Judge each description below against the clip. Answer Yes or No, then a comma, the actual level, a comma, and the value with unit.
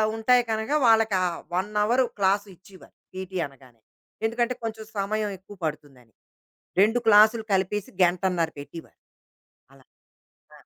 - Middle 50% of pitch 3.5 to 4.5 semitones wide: Yes, average, 4.0 semitones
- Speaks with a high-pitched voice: Yes, high, 200 Hz